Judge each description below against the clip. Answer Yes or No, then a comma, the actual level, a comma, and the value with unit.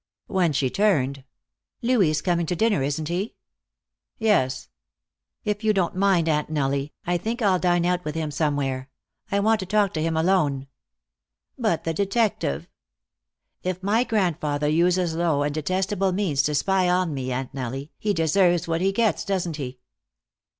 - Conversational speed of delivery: Yes, average, 165 wpm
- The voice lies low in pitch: No, medium, 175 Hz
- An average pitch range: Yes, average, 4.8 semitones